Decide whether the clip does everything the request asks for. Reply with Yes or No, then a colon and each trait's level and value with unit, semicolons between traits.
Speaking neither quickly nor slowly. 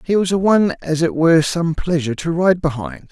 No: fast, 230 wpm